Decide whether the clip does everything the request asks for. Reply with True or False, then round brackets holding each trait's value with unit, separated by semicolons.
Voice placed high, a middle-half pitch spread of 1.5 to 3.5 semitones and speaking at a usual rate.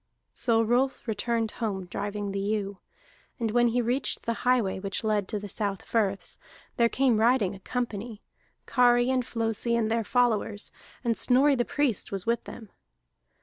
True (225 Hz; 2.9 semitones; 170 wpm)